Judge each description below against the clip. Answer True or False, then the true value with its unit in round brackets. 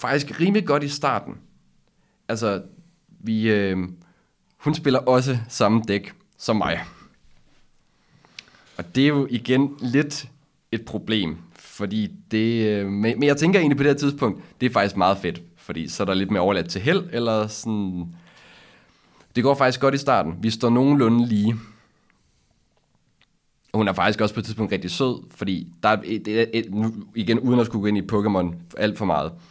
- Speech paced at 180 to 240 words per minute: False (170 wpm)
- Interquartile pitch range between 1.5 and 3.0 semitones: False (5.1 semitones)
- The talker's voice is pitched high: False (115 Hz)